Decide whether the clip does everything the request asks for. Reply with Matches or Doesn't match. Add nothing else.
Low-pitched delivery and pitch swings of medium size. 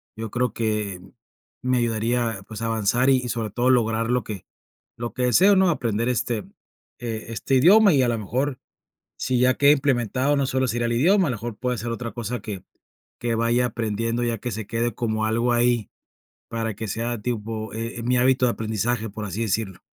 Doesn't match